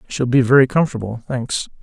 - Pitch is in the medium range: No, low, 125 Hz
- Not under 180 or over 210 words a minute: Yes, average, 200 wpm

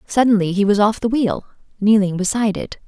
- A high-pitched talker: Yes, high, 210 Hz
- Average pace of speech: Yes, average, 190 wpm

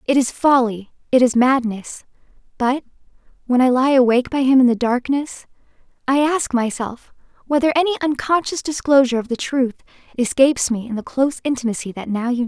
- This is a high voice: Yes, very high, 255 Hz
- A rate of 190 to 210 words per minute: No, average, 175 wpm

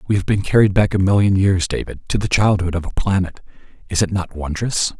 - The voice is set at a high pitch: No, very low, 95 Hz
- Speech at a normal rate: No, fast, 215 wpm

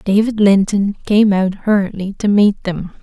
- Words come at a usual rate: Yes, average, 160 wpm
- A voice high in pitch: Yes, high, 200 Hz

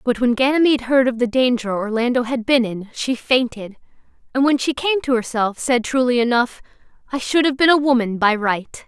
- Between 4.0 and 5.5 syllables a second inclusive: Yes, 5.3 syllables/s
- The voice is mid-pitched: No, very high, 250 Hz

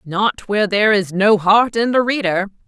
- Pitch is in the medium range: No, high, 205 Hz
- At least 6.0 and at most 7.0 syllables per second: No, 5.0 syllables/s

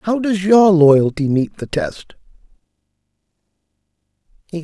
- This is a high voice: No, medium, 175 Hz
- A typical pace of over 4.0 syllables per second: No, 3.7 syllables/s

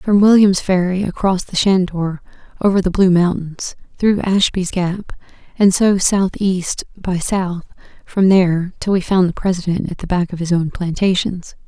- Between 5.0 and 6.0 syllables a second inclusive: No, 4.7 syllables/s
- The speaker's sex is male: No, female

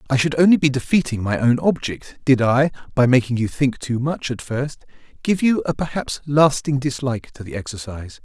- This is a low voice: Yes, low, 130 Hz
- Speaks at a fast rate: No, average, 195 wpm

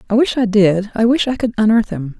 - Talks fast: Yes, fast, 275 wpm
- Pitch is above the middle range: Yes, high, 220 Hz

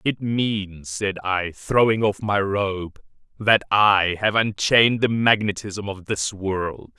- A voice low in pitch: Yes, low, 100 Hz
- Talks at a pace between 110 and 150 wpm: Yes, average, 145 wpm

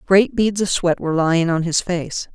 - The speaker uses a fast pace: Yes, fast, 230 wpm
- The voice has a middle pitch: Yes, medium, 180 Hz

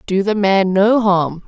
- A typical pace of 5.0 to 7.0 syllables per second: No, 3.8 syllables/s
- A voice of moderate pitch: No, high, 195 Hz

